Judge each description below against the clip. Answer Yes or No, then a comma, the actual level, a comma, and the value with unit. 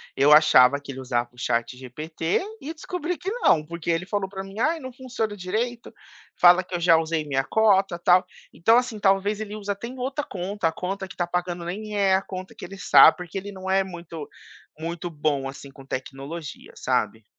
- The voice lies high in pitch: No, medium, 180 Hz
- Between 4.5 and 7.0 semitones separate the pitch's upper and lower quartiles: Yes, average, 4.9 semitones